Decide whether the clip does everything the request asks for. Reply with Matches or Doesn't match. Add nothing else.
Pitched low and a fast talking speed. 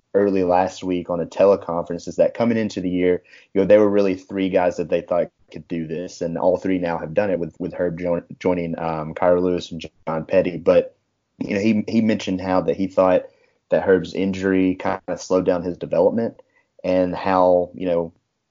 Matches